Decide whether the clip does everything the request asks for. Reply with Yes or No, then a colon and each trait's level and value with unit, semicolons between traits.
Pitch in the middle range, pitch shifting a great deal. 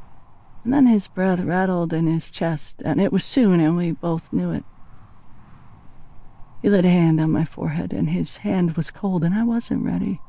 No: medium, 180 Hz; average, 3.8 semitones